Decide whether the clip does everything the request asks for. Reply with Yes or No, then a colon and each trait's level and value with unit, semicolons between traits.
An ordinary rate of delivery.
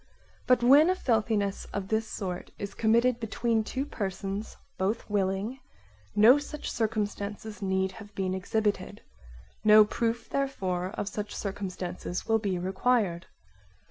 No: slow, 130 wpm